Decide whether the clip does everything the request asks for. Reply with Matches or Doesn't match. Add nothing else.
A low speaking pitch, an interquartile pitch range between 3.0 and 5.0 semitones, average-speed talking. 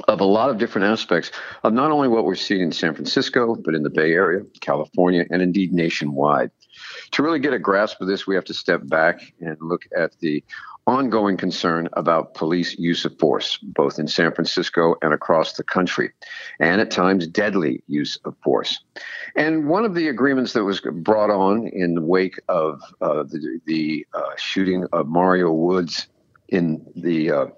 Doesn't match